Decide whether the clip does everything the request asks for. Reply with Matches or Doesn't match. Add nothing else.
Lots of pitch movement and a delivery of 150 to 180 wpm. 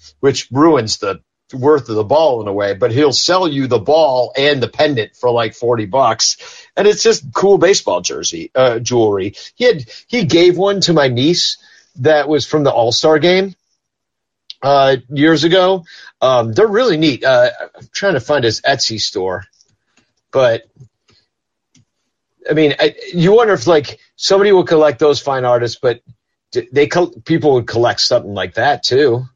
Matches